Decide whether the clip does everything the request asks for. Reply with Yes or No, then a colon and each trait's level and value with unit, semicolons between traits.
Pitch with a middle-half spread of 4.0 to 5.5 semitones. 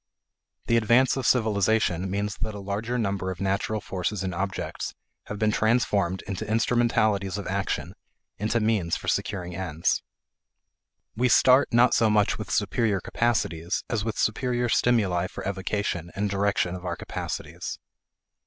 No: average, 2.9 semitones